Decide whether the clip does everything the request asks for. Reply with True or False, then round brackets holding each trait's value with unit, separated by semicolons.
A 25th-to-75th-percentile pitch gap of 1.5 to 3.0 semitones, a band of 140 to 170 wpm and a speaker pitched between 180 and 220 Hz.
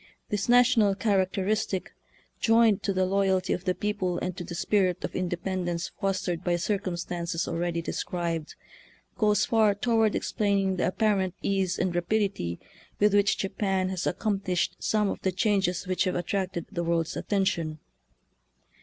True (2.5 semitones; 150 wpm; 190 Hz)